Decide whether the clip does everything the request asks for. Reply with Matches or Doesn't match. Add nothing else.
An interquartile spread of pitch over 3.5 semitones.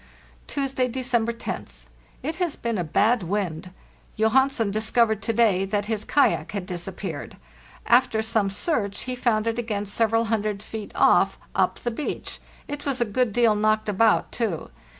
Doesn't match